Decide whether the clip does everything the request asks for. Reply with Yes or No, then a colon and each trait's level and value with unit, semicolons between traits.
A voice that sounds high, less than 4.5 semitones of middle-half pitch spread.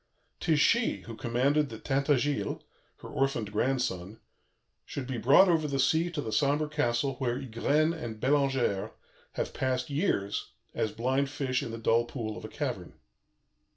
No: low, 135 Hz; average, 3.8 semitones